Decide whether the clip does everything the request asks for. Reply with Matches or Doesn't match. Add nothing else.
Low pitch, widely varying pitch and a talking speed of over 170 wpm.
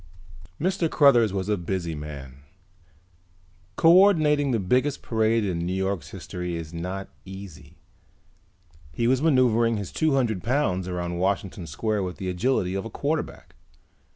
Doesn't match